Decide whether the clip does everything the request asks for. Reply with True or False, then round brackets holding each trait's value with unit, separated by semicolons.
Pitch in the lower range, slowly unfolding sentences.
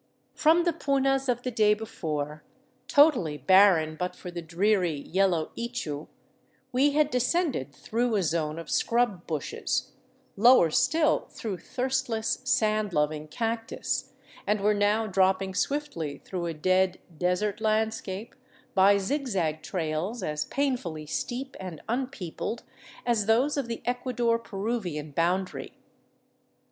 False (205 Hz; 125 wpm)